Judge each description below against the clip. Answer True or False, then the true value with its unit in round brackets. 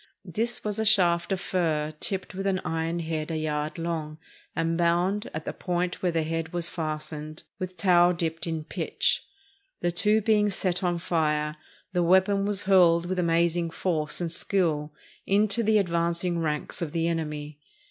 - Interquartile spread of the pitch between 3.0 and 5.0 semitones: False (2.6 semitones)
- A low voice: False (170 Hz)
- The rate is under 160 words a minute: False (175 wpm)